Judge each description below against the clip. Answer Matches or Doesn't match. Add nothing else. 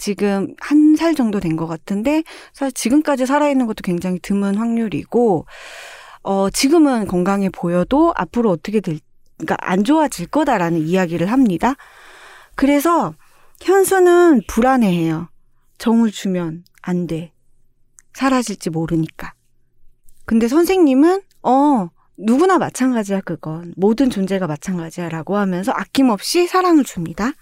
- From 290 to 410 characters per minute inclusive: Matches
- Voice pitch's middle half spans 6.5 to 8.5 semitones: Matches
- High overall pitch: Matches